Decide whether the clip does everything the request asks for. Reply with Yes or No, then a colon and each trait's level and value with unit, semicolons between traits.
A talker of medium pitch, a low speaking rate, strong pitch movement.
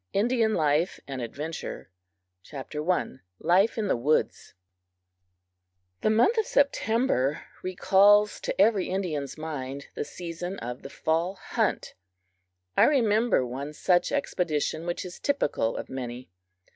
Yes: medium, 175 Hz; slow, 120 wpm; wide, 6.7 semitones